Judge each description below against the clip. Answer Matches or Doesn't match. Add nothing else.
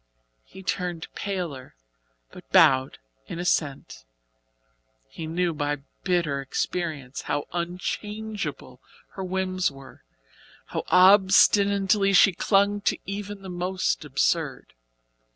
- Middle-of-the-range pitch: Matches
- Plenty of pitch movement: Doesn't match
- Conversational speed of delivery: Doesn't match